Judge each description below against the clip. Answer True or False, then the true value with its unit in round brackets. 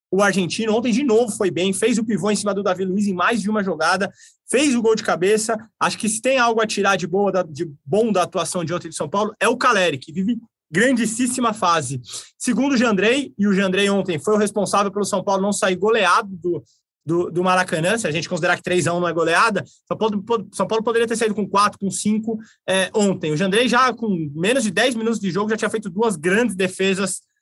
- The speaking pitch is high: True (200 Hz)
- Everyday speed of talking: False (235 wpm)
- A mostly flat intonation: False (3.6 semitones)